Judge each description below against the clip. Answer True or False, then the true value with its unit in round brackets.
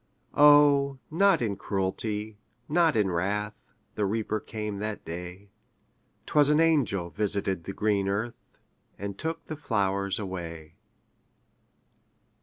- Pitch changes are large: True (6.2 semitones)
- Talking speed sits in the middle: False (115 wpm)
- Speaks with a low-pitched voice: True (105 Hz)